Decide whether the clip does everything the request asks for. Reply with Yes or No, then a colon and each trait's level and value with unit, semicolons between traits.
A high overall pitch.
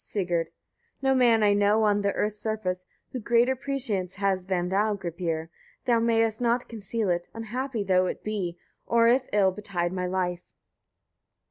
Yes: high, 205 Hz